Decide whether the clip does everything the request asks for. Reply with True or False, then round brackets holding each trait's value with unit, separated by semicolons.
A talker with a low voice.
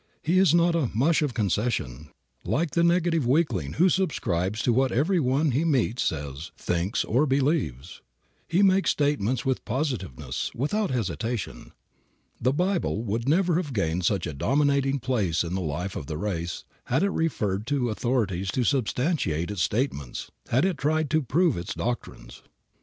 True (125 Hz)